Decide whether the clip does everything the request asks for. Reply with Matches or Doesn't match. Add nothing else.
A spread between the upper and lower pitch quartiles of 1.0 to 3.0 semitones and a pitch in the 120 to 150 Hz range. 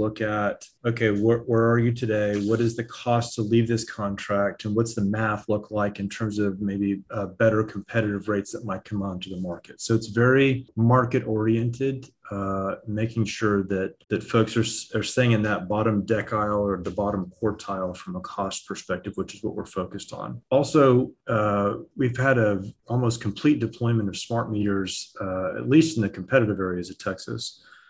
Doesn't match